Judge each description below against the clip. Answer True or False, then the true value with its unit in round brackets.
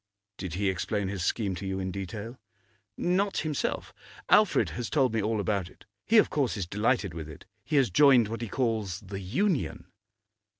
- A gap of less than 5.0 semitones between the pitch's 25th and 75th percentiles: False (5.5 semitones)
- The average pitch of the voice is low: True (105 Hz)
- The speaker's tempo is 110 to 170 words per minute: False (185 wpm)